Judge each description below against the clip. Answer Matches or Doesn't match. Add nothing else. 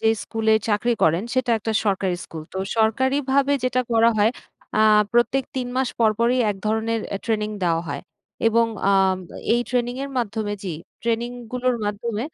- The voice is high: Matches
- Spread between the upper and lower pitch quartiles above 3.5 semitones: Doesn't match